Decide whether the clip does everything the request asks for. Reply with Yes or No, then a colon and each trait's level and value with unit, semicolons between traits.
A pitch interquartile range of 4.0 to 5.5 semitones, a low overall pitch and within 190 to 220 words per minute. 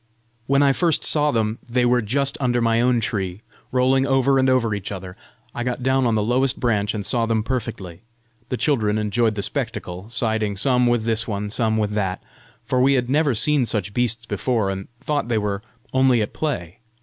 No: average, 3.5 semitones; low, 115 Hz; average, 200 wpm